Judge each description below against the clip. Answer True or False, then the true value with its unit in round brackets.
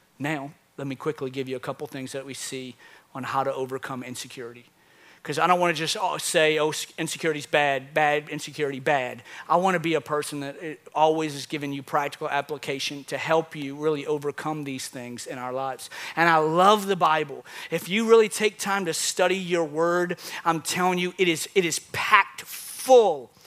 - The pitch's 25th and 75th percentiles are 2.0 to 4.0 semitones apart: True (3.4 semitones)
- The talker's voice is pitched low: False (150 Hz)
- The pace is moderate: True (195 wpm)